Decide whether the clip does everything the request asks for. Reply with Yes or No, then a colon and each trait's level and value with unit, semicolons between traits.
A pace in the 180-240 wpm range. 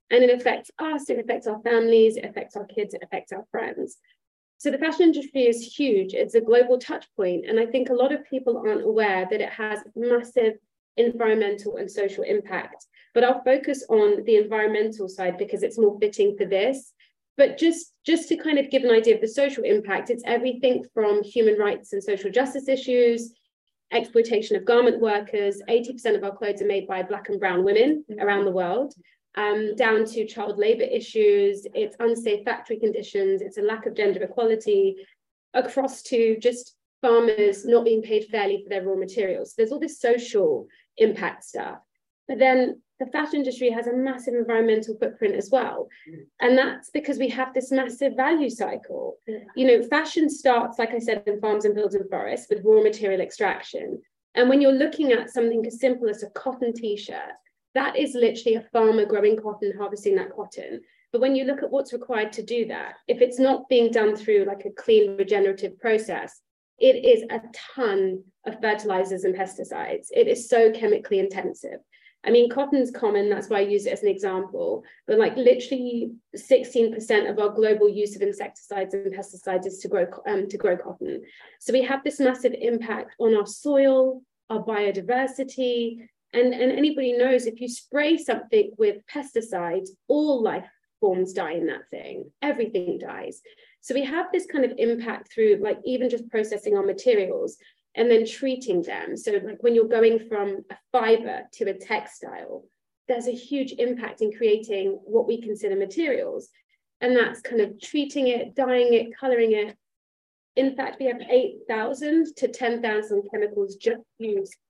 Yes: average, 185 wpm